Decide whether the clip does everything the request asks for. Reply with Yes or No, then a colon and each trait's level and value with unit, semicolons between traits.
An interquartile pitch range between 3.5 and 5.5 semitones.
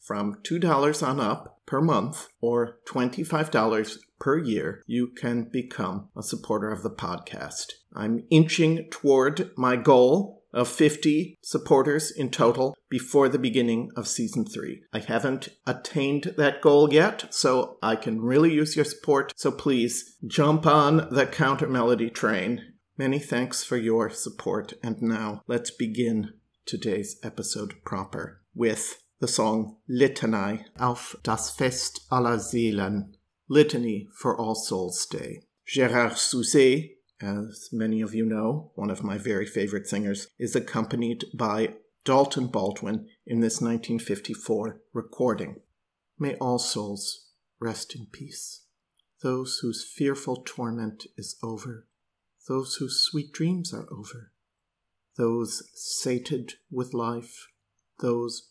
Yes: average, 3.9 semitones